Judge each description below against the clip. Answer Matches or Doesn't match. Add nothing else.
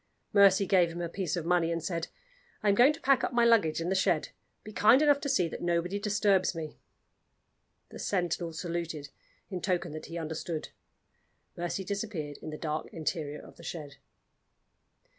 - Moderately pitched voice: Matches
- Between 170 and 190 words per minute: Matches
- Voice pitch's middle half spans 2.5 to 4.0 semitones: Matches